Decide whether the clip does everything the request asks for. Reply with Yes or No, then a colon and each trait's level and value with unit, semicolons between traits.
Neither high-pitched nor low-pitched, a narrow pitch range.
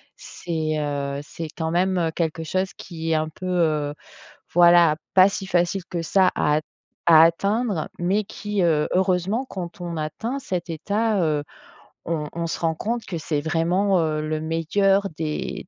No: medium, 170 Hz; average, 3.2 semitones